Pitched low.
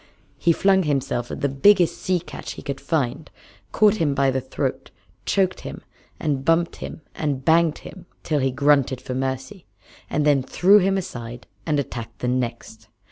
No: medium, 145 Hz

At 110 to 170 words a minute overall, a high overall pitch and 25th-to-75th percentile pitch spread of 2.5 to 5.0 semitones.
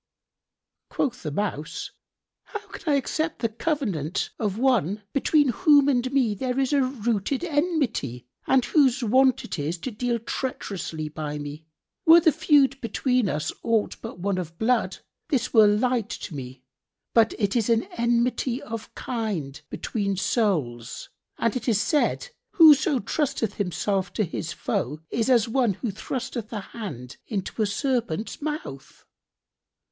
No: average, 150 wpm; high, 230 Hz; wide, 5.6 semitones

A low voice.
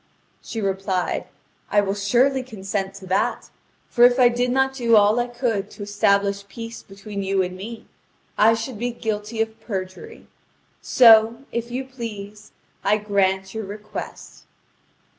No: high, 215 Hz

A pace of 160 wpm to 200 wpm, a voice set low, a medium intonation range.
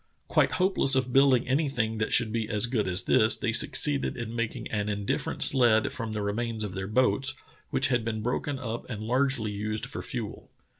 Yes: average, 195 wpm; low, 115 Hz; average, 3.3 semitones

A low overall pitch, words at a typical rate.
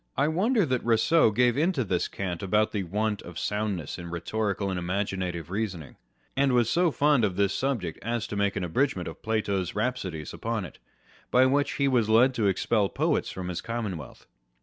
Yes: low, 105 Hz; average, 195 wpm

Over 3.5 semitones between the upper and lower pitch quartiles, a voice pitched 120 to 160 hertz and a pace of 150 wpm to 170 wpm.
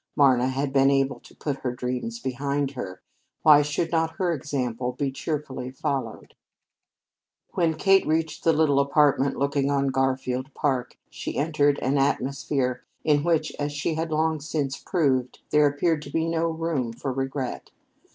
No: average, 2.7 semitones; medium, 140 Hz; average, 160 wpm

